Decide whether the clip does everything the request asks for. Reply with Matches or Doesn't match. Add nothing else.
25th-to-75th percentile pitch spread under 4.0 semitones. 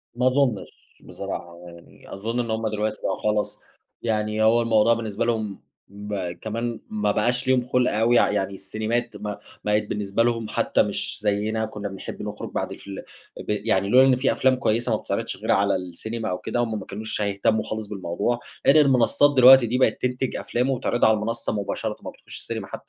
Matches